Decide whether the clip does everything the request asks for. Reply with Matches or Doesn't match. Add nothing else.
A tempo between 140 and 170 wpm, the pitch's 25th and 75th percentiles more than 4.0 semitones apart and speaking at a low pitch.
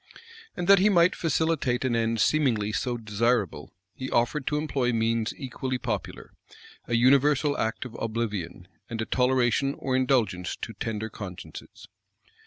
Doesn't match